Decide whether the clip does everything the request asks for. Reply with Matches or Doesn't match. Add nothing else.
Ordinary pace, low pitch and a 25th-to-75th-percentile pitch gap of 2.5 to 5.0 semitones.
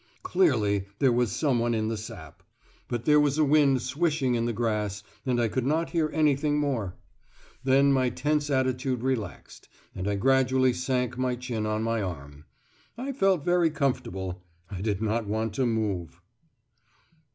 Matches